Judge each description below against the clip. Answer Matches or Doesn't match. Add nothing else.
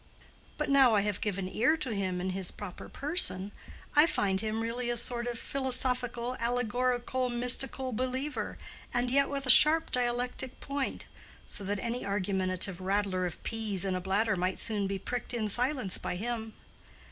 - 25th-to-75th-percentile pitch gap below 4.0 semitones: Doesn't match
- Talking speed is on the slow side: Doesn't match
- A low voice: Doesn't match